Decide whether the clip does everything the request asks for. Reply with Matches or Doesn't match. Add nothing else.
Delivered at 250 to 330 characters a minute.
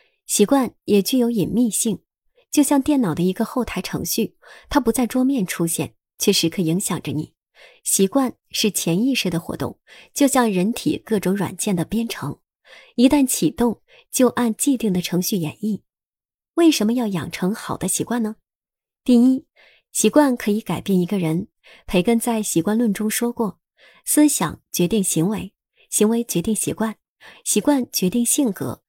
Doesn't match